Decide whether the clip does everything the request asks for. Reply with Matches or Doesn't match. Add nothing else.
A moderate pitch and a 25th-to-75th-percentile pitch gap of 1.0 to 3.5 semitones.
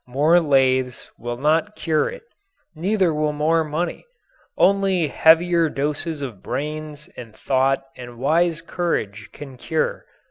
Doesn't match